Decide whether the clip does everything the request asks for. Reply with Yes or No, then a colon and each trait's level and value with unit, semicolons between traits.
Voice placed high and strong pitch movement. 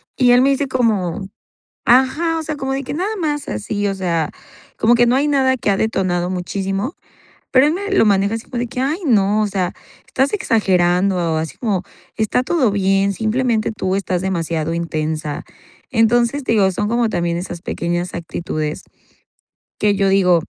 Yes: high, 205 Hz; wide, 6.2 semitones